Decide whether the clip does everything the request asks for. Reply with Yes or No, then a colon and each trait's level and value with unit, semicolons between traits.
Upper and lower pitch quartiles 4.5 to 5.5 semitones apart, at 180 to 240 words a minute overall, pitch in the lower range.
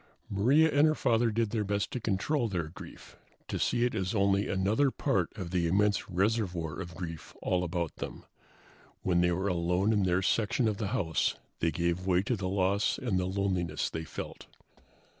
No: average, 3.8 semitones; average, 190 wpm; very low, 95 Hz